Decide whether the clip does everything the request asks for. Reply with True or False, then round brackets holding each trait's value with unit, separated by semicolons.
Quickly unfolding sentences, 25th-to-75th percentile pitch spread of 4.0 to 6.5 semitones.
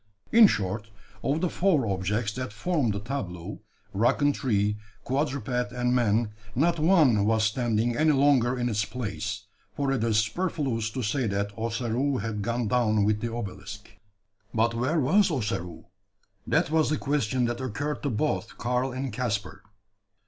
False (160 wpm; 4.3 semitones)